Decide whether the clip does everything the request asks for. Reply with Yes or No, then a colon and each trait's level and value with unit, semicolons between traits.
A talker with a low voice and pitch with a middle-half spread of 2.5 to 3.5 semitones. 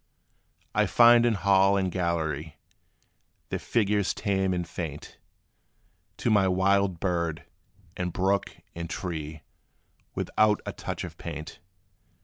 Yes: very low, 95 Hz; average, 3.0 semitones